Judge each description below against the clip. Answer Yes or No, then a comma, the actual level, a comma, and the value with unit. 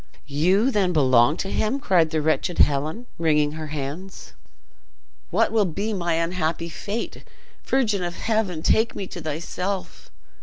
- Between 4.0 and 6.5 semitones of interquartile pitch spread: Yes, average, 4.4 semitones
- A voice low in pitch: No, medium, 175 Hz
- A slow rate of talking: No, average, 145 wpm